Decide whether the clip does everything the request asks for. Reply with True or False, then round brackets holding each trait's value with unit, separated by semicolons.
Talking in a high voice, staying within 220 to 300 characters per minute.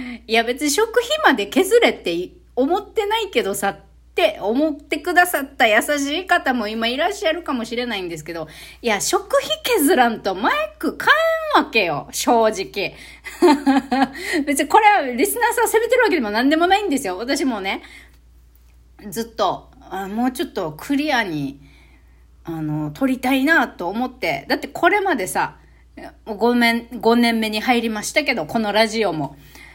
False (265 Hz; 315 characters per minute)